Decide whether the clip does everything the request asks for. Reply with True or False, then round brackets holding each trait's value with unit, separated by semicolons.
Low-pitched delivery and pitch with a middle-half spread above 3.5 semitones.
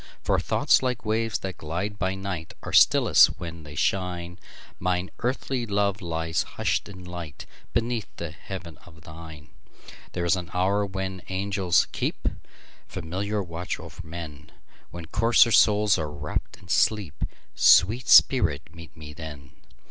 True (90 Hz; 3.9 semitones)